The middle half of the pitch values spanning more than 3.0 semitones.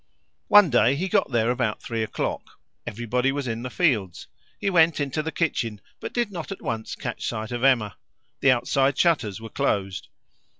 Yes: wide, 5.4 semitones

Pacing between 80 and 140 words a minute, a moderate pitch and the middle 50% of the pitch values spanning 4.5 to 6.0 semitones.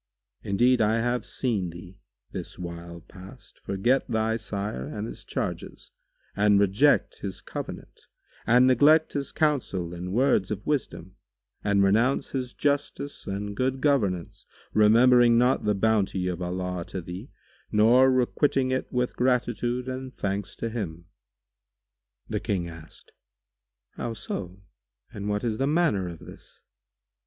No: slow, 135 wpm; low, 110 Hz; average, 5.0 semitones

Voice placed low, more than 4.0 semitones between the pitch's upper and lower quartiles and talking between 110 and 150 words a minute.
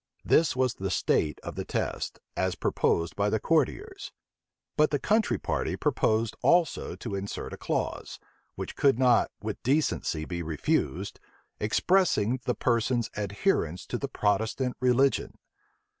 Yes: low, 120 Hz; wide, 5.5 semitones; average, 140 wpm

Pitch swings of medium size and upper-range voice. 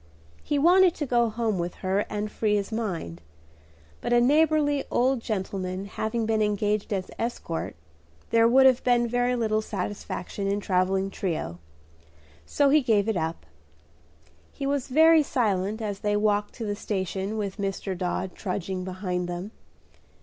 Yes: average, 4.0 semitones; high, 210 Hz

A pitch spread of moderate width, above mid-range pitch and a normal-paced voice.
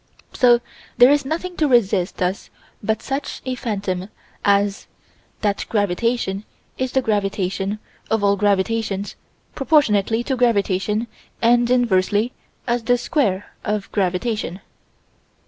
No: average, 3.7 semitones; high, 215 Hz; slow, 115 wpm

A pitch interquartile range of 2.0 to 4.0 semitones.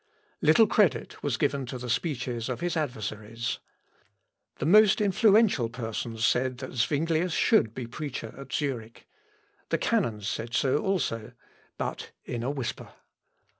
No: wide, 5.5 semitones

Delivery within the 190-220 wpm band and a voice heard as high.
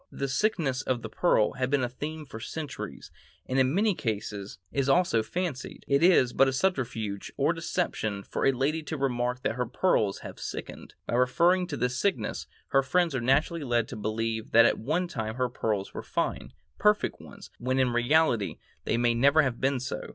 No: average, 195 wpm; low, 130 Hz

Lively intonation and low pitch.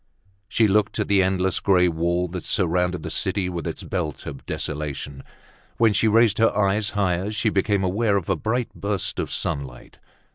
No: average, 3.1 semitones; very low, 95 Hz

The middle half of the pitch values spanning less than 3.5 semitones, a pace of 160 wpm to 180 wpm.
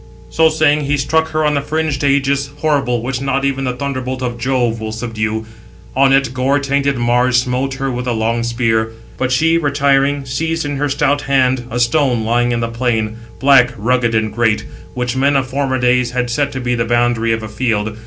No: average, 2.8 semitones; fast, 205 wpm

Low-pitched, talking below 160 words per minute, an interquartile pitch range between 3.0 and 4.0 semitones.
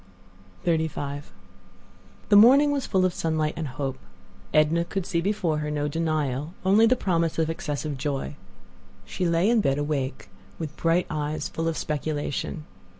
No: medium, 160 Hz; average, 150 wpm; average, 3.3 semitones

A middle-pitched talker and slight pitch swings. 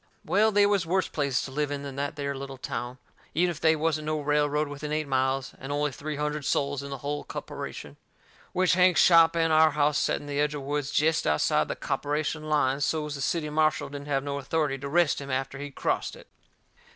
Yes: medium, 145 Hz; narrow, 1.9 semitones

